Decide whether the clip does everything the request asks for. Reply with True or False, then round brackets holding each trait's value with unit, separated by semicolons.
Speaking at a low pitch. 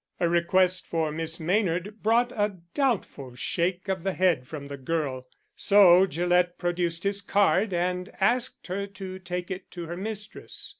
False (180 Hz)